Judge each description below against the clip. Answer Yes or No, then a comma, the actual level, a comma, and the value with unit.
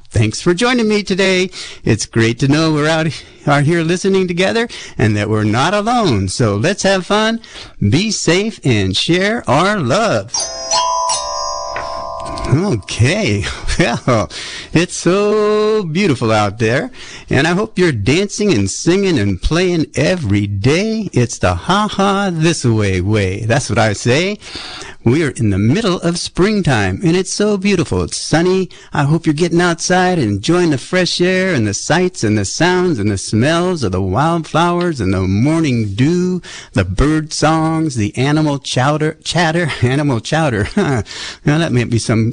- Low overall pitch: No, medium, 155 Hz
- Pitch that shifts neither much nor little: No, wide, 8.5 semitones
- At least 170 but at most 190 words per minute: No, average, 160 wpm